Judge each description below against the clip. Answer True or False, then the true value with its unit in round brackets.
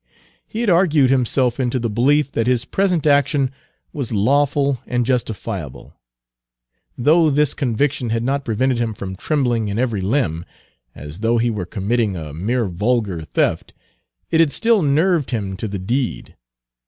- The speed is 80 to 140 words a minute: False (155 wpm)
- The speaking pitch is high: False (125 Hz)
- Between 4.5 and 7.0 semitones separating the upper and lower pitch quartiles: True (4.8 semitones)